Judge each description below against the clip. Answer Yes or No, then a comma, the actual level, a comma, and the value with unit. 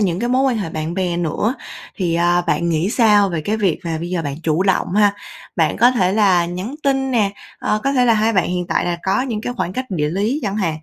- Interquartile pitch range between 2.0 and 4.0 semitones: No, average, 4.6 semitones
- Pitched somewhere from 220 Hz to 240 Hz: No, high, 195 Hz